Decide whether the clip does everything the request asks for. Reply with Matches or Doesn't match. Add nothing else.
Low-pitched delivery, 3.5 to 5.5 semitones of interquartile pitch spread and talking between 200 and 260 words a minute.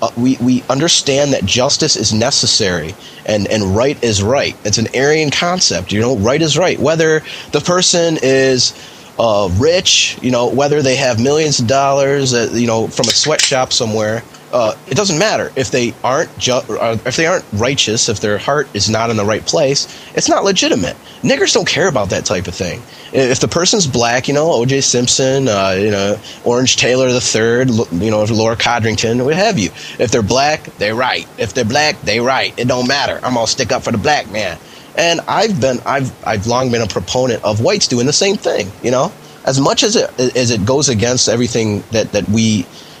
Matches